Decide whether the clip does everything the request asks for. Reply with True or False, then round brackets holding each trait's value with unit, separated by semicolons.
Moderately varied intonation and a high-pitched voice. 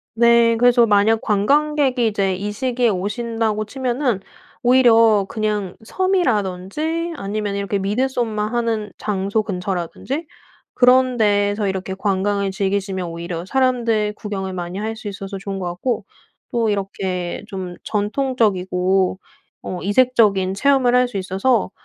True (3.9 semitones; 210 Hz)